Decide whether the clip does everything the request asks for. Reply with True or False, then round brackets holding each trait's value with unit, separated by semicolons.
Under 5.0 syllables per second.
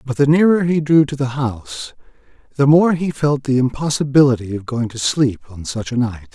False (5.4 syllables/s)